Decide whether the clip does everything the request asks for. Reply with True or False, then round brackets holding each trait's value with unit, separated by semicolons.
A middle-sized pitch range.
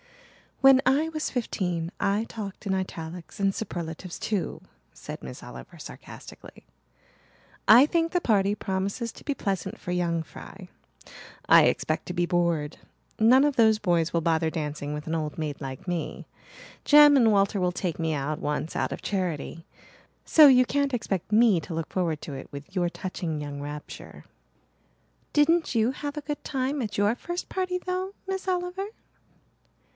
False (8.3 semitones)